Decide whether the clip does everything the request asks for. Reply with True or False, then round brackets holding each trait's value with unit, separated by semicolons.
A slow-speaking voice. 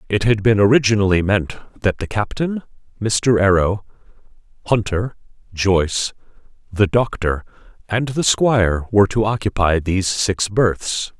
True (125 wpm)